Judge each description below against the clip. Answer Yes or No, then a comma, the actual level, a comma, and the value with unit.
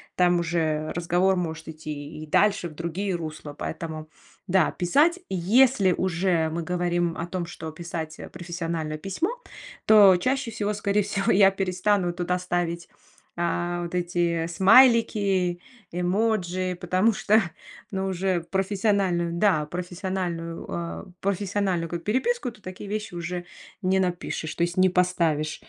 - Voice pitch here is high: No, medium, 180 Hz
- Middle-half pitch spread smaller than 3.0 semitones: Yes, narrow, 2.4 semitones